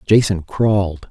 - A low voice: Yes, low, 100 Hz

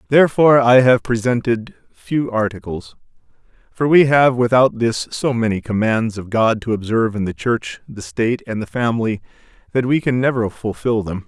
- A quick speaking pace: No, average, 170 wpm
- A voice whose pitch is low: Yes, low, 115 Hz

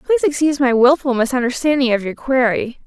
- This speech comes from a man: No, female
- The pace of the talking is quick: No, average, 165 wpm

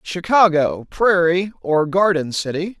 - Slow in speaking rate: Yes, slow, 105 wpm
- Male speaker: Yes, male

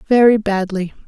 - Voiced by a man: No, female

